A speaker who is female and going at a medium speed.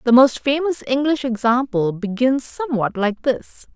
Yes: female; average, 145 wpm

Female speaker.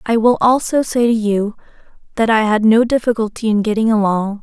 Yes: female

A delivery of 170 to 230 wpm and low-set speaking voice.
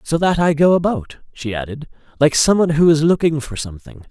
No: fast, 205 wpm; medium, 150 Hz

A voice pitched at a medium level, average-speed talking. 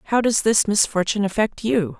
No: high, 210 Hz; average, 180 wpm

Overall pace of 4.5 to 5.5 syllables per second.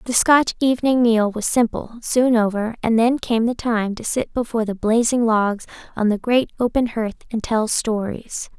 Yes: 4.7 syllables/s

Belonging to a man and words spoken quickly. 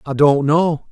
No: male; average, 195 wpm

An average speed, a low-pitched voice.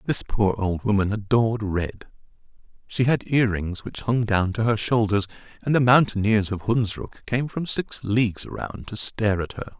Yes: average, 180 wpm; low, 110 Hz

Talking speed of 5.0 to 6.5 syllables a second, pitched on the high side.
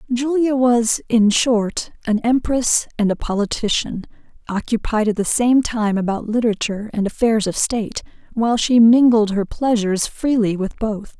No: 4.7 syllables/s; high, 225 Hz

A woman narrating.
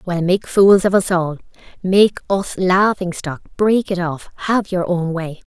Yes: female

